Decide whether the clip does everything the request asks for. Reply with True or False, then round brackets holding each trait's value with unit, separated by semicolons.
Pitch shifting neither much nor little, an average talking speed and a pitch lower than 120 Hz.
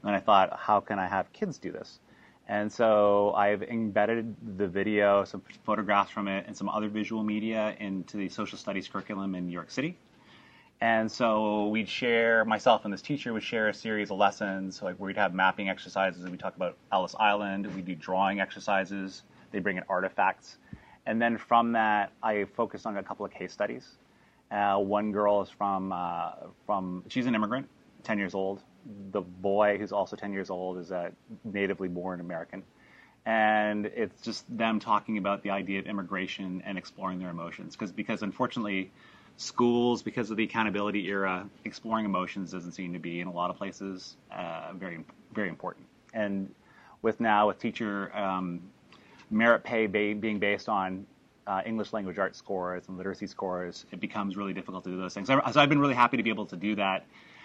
False (2.1 semitones; 185 wpm; 100 Hz)